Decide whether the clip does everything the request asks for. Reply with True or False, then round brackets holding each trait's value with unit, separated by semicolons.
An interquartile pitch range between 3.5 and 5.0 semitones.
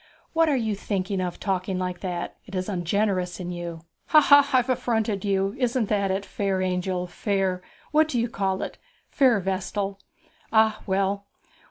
False (3.0 semitones)